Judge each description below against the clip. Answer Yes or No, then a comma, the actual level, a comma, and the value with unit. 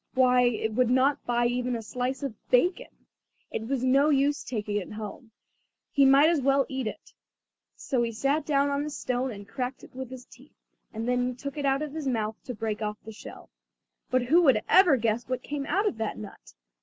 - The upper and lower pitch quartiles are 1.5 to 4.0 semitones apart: Yes, average, 3.3 semitones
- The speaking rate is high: Yes, fast, 215 wpm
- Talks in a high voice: Yes, very high, 255 Hz